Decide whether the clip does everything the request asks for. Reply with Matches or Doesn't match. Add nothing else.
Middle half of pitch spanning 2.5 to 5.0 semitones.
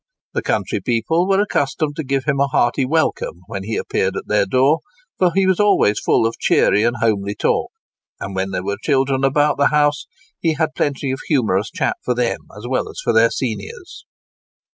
Doesn't match